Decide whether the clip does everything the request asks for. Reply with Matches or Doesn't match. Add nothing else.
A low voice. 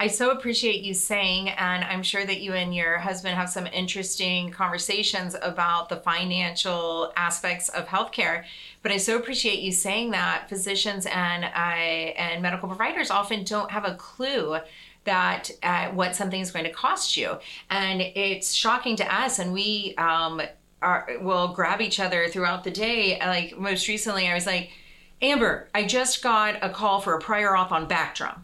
Doesn't match